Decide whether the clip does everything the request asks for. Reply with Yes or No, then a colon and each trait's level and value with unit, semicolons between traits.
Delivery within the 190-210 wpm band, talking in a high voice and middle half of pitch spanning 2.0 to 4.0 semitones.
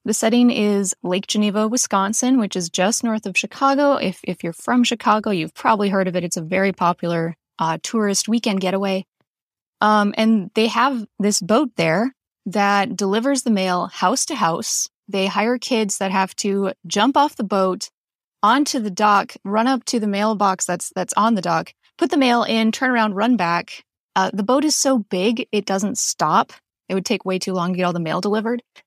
Yes: average, 200 wpm; high, 205 Hz; average, 3.7 semitones